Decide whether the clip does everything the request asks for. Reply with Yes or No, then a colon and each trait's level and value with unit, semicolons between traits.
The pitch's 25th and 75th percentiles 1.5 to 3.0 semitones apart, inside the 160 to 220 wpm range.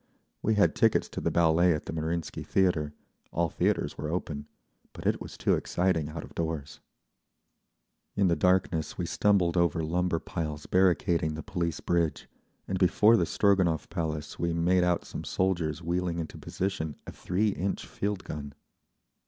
No: narrow, 2.6 semitones; average, 150 wpm